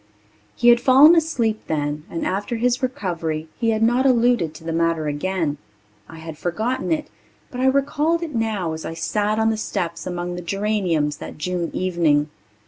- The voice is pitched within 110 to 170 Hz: No, high, 190 Hz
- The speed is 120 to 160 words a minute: No, average, 180 wpm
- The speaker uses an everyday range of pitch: No, wide, 6.6 semitones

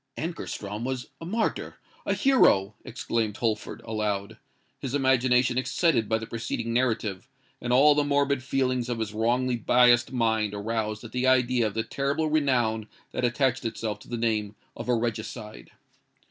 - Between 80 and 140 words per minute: No, average, 155 wpm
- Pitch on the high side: No, low, 120 Hz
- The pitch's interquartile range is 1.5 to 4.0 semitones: Yes, average, 2.9 semitones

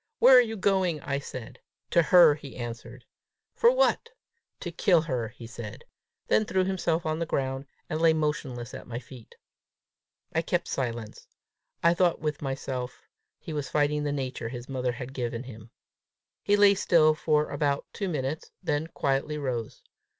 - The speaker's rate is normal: Yes, average, 165 wpm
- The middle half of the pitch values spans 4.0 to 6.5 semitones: Yes, average, 4.9 semitones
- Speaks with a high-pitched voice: No, medium, 145 Hz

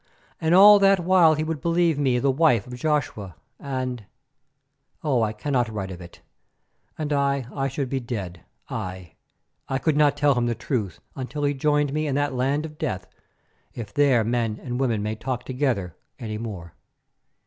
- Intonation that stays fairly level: No, average, 4.5 semitones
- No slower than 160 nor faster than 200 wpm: Yes, average, 175 wpm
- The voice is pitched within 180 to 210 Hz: No, low, 135 Hz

